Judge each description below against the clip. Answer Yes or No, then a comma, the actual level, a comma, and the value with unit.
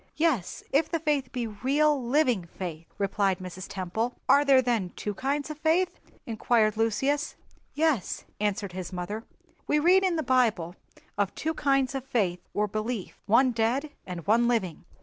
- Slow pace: No, average, 160 wpm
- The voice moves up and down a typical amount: No, wide, 6.2 semitones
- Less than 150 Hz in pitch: No, high, 235 Hz